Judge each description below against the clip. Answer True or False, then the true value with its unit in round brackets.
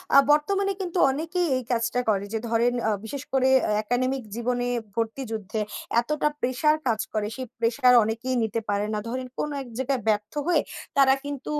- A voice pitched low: False (250 Hz)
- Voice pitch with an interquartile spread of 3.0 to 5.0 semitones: True (3.6 semitones)